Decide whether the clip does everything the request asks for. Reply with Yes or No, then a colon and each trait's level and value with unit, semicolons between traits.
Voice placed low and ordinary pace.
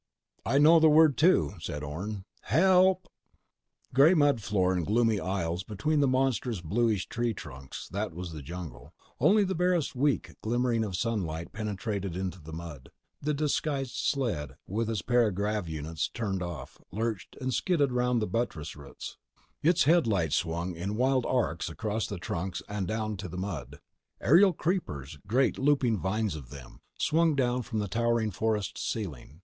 Yes: low, 110 Hz; average, 145 wpm